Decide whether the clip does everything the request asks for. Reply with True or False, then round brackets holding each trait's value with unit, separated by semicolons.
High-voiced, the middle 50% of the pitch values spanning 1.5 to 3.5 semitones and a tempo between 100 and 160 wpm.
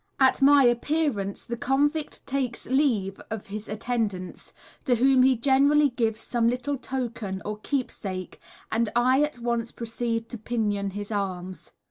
False (235 Hz; 4.0 semitones; 145 wpm)